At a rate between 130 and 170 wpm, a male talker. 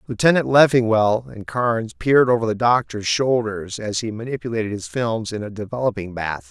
Yes: average, 165 wpm; male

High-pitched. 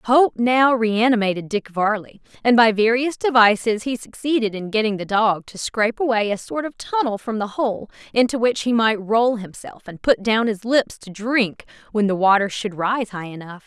Yes: high, 220 Hz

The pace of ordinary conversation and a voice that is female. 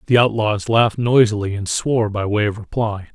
No: average, 190 wpm; male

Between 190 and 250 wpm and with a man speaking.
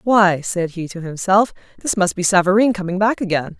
No: average, 200 wpm; female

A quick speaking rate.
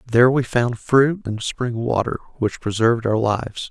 No: average, 180 wpm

